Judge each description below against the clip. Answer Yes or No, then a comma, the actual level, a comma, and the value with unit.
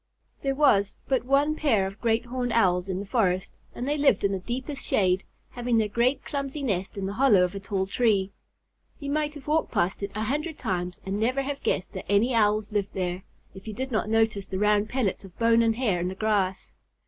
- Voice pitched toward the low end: No, high, 215 Hz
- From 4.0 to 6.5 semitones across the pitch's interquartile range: Yes, average, 5.0 semitones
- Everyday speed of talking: No, fast, 225 wpm